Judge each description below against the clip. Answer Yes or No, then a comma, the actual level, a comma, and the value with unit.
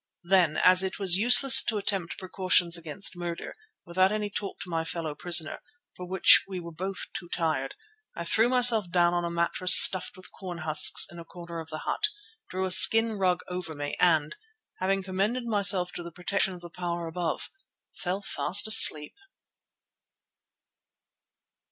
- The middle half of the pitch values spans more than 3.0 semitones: No, narrow, 2.4 semitones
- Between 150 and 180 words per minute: Yes, average, 170 wpm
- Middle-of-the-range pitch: Yes, medium, 180 Hz